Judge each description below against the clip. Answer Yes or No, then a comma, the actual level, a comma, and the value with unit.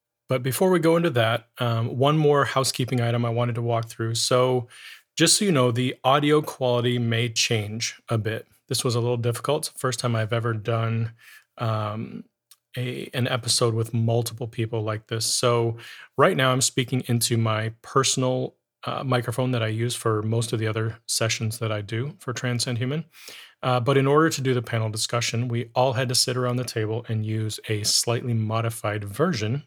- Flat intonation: Yes, narrow, 2.2 semitones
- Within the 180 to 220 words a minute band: Yes, average, 190 wpm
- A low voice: Yes, low, 120 Hz